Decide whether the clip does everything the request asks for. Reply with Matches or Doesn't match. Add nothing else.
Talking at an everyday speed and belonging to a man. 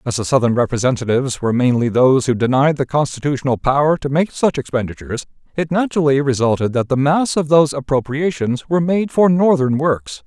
Matches